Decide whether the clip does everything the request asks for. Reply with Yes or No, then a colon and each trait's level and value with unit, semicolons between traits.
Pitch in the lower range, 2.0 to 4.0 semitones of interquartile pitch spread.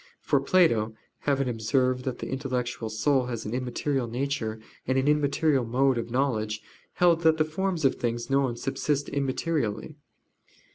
Yes: low, 130 Hz; average, 3.5 semitones